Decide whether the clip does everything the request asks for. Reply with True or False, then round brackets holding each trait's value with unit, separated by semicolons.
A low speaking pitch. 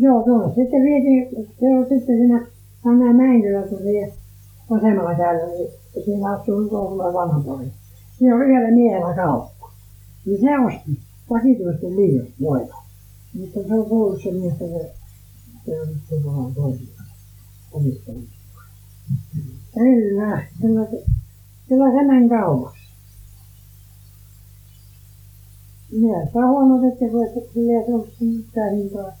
False (175 Hz)